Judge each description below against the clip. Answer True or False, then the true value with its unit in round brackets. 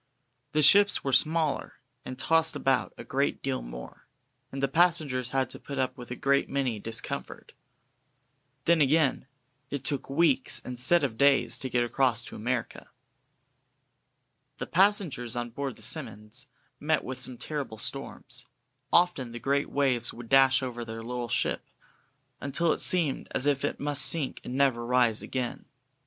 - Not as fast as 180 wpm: True (160 wpm)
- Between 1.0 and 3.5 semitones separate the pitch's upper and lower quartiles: True (2.9 semitones)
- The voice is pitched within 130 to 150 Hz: True (135 Hz)